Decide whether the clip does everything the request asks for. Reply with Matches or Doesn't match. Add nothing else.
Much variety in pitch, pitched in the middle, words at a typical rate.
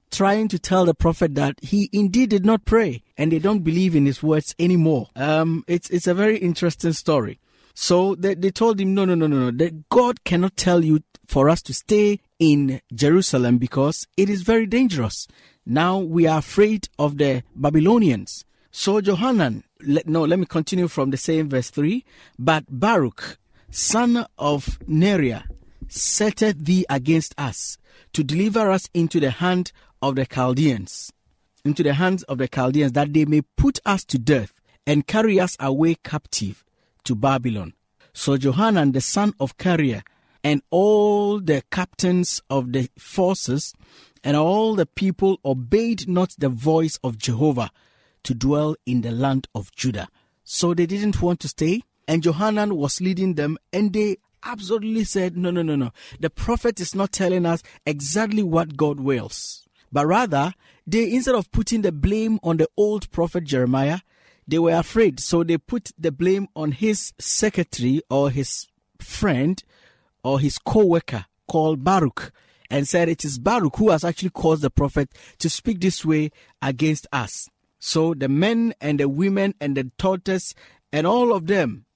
Matches